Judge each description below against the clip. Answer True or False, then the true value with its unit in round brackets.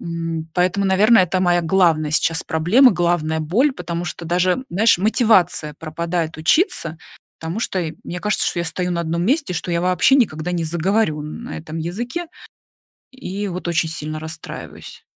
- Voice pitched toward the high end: False (175 Hz)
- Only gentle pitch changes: False (3.4 semitones)